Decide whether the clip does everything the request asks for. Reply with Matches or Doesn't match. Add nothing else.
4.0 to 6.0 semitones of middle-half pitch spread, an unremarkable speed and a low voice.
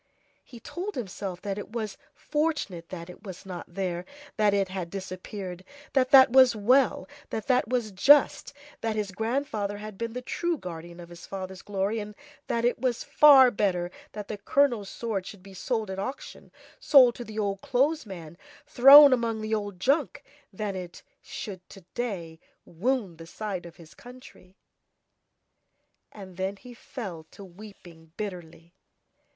Doesn't match